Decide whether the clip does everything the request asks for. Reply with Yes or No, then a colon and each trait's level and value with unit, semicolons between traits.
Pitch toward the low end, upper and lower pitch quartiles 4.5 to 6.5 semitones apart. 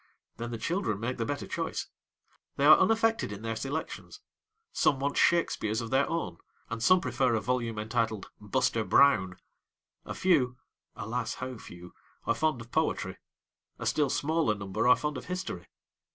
Yes: low, 125 Hz; average, 5.2 semitones